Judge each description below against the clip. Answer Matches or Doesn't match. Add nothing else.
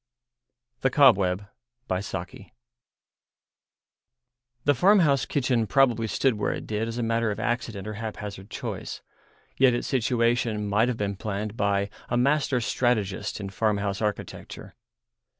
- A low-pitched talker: Matches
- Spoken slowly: Matches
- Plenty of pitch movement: Doesn't match